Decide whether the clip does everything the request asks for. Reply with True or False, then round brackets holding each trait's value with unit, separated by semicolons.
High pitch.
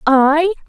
True (310 Hz)